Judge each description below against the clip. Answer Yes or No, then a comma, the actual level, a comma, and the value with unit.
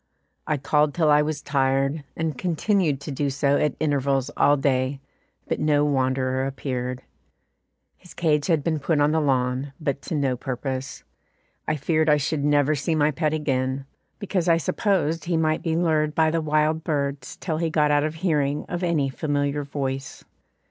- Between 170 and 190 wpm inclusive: Yes, average, 175 wpm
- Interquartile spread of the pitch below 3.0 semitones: Yes, narrow, 2.4 semitones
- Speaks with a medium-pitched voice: Yes, medium, 145 Hz